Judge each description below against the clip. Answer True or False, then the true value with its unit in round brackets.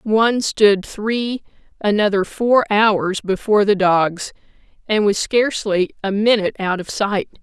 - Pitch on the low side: False (205 Hz)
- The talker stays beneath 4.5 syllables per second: True (4.2 syllables/s)